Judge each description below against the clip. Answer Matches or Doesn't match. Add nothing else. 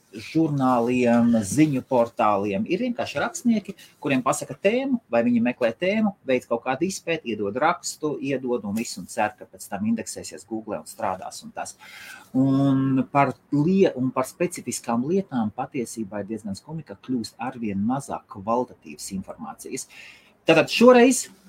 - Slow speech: Matches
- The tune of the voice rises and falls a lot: Matches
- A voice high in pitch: Doesn't match